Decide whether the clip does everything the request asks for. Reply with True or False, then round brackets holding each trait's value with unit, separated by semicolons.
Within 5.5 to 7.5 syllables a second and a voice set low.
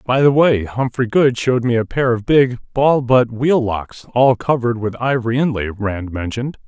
False (5.1 syllables/s; 120 Hz)